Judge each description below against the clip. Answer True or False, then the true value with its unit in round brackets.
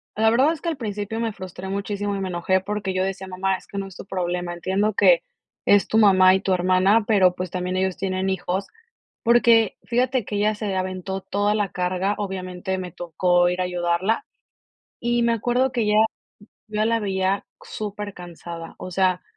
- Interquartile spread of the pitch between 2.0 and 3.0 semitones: True (2.4 semitones)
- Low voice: False (195 Hz)